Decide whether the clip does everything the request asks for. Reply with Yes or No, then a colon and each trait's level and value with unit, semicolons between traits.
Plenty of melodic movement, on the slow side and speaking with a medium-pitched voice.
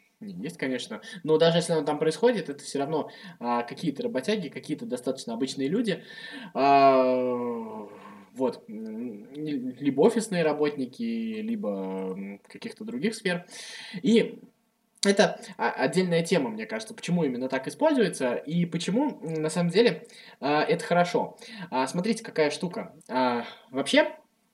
No: wide, 8.3 semitones; average, 125 wpm; medium, 180 Hz